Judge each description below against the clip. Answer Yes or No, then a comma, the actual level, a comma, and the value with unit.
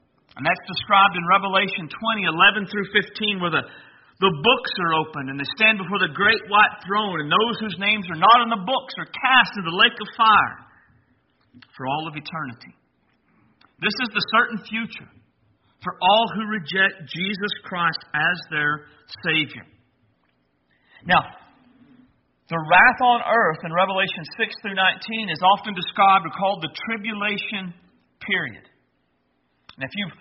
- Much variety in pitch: No, average, 5.0 semitones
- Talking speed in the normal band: Yes, average, 155 wpm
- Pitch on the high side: Yes, high, 195 Hz